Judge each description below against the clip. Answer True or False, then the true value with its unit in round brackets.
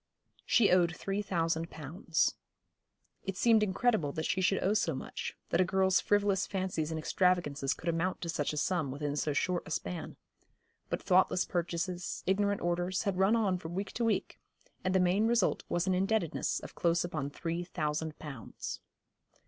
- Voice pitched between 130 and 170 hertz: False (180 Hz)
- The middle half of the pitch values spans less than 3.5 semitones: True (2.9 semitones)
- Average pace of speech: True (175 wpm)